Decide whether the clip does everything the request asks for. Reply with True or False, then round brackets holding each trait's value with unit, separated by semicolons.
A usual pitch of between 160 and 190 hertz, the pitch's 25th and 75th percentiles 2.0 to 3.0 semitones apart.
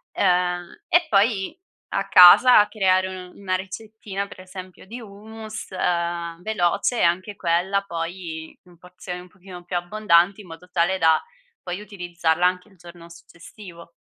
True (185 Hz; 2.4 semitones)